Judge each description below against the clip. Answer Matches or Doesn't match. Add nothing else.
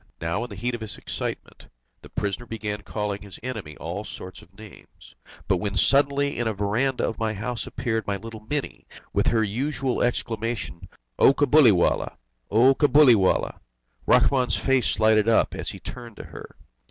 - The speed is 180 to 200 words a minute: Doesn't match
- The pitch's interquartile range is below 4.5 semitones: Matches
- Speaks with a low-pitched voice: Matches